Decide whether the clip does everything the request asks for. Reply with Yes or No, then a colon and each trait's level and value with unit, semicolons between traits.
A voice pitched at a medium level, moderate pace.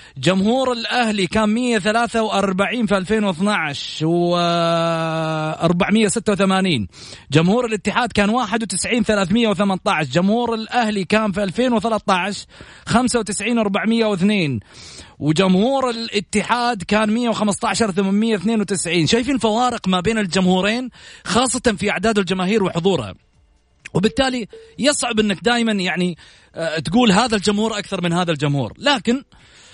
No: high, 210 Hz; average, 95 wpm